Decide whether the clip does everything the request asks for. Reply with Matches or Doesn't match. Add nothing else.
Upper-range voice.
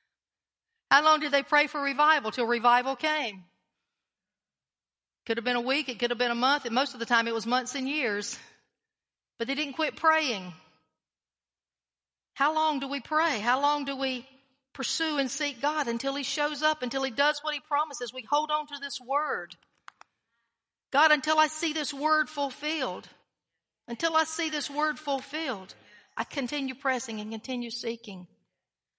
Matches